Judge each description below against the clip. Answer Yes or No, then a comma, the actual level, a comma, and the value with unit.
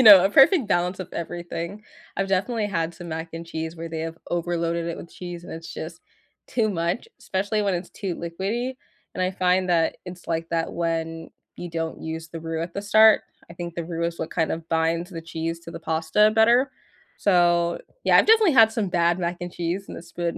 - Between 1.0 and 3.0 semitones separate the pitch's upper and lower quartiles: Yes, average, 2.7 semitones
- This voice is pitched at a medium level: Yes, medium, 170 Hz